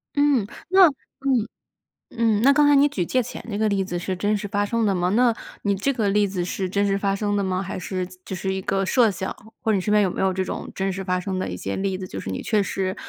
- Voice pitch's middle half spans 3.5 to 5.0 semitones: No, average, 2.7 semitones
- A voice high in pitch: Yes, high, 200 Hz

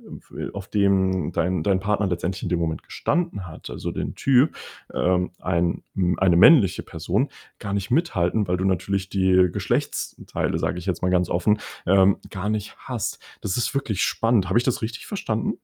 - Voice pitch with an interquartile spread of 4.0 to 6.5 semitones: No, average, 2.7 semitones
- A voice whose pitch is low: Yes, very low, 95 Hz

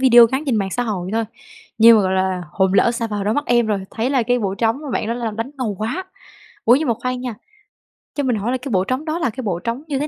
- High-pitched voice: Yes, high, 230 Hz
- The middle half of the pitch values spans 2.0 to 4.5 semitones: Yes, average, 3.5 semitones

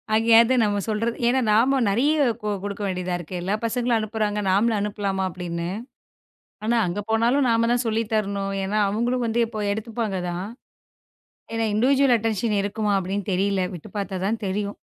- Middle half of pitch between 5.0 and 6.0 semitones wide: No, average, 2.7 semitones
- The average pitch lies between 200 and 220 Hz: Yes, high, 215 Hz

